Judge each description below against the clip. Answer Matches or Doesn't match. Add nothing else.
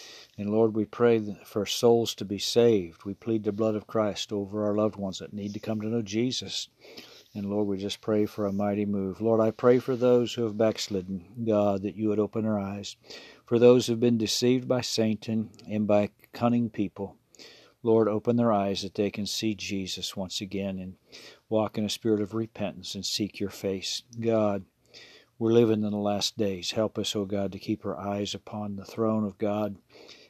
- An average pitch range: Doesn't match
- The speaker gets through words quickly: Matches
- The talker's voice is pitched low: Matches